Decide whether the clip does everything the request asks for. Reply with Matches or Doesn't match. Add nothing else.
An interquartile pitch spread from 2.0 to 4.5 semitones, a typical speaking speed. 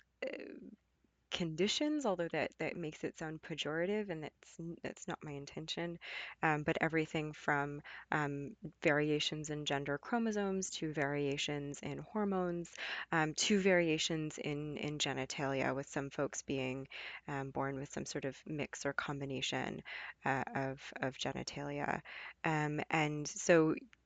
Doesn't match